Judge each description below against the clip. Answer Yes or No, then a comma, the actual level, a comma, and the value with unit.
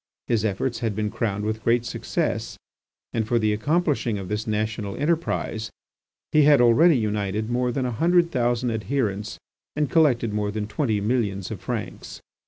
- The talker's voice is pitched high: No, low, 115 Hz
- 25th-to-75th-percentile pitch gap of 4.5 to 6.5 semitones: No, average, 3.4 semitones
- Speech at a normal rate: Yes, average, 165 wpm